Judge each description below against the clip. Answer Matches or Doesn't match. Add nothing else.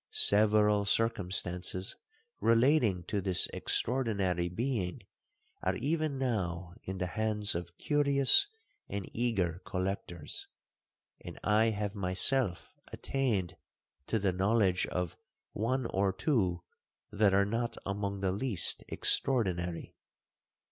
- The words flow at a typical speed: Doesn't match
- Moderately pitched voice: Doesn't match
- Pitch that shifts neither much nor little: Matches